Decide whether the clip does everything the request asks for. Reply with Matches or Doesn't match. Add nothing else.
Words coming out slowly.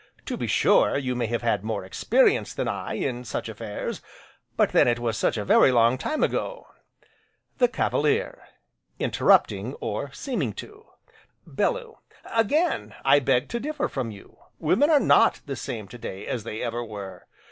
Doesn't match